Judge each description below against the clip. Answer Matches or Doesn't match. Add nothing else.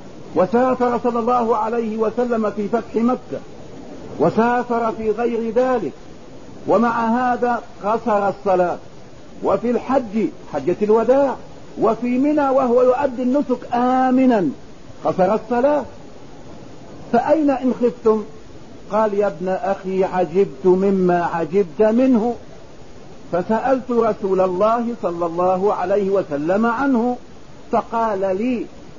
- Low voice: Doesn't match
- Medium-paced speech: Doesn't match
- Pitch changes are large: Doesn't match